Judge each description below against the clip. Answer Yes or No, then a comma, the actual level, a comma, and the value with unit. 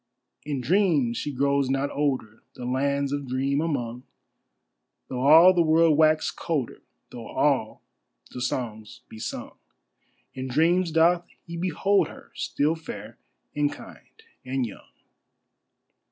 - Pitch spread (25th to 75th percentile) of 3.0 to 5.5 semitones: Yes, average, 4.1 semitones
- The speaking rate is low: Yes, slow, 130 wpm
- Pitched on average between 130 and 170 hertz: Yes, medium, 140 Hz